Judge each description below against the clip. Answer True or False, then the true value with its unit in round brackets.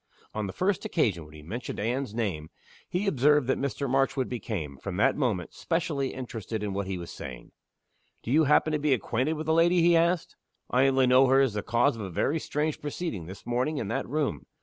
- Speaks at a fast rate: True (215 wpm)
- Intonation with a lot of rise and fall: True (6.4 semitones)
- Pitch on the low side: True (130 Hz)